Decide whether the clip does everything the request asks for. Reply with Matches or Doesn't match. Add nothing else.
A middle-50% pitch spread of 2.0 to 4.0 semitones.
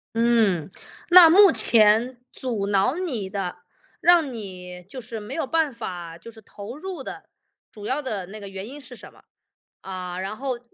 Doesn't match